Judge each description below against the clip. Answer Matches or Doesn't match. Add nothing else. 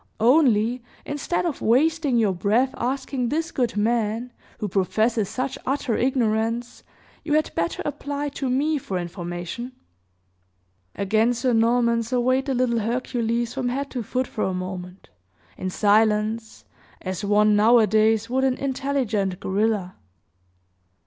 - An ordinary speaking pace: Doesn't match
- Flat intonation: Doesn't match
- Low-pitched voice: Doesn't match